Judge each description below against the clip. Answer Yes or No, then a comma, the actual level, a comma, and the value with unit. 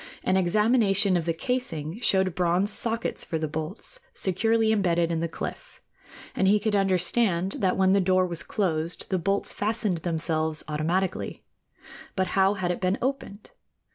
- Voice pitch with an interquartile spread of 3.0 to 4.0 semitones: Yes, average, 3.4 semitones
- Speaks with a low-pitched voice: No, high, 190 Hz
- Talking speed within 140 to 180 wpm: Yes, average, 160 wpm